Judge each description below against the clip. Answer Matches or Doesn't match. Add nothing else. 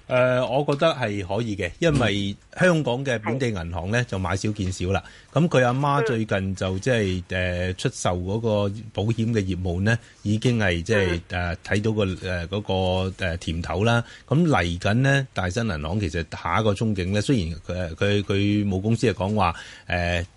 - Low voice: Matches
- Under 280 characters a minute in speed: Matches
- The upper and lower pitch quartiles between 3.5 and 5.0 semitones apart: Matches